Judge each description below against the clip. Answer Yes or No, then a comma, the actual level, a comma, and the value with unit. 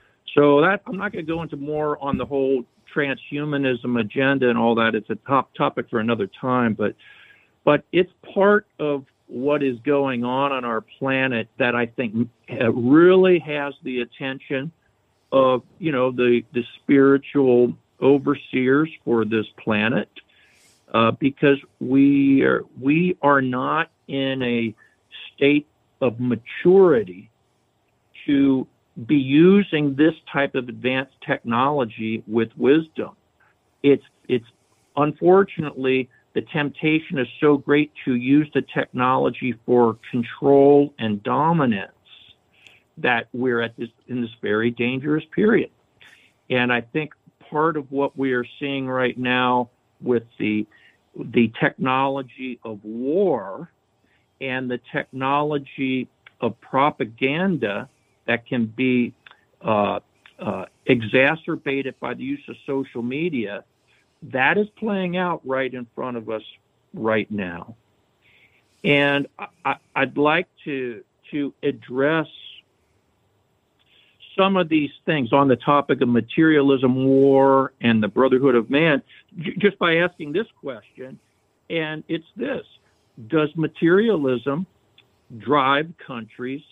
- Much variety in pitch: No, average, 3.5 semitones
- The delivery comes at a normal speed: No, slow, 125 wpm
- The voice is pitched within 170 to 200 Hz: No, low, 135 Hz